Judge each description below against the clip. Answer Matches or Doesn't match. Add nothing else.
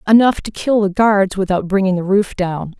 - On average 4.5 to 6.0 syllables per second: Matches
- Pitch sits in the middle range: Doesn't match